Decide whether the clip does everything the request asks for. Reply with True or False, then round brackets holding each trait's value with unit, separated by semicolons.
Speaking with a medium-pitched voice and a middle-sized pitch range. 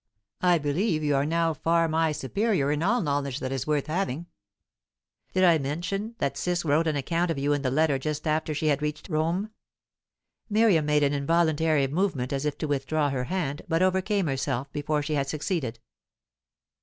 True (155 Hz; 3.1 semitones)